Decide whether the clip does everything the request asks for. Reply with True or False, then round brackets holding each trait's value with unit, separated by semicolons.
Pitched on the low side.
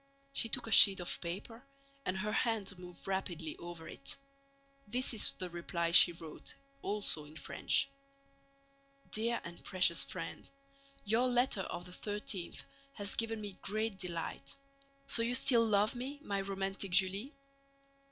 False (200 Hz)